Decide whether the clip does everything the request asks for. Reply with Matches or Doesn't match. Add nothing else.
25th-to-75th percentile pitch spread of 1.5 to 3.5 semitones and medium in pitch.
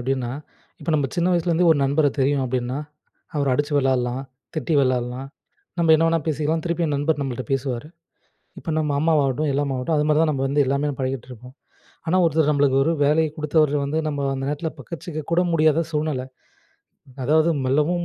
Matches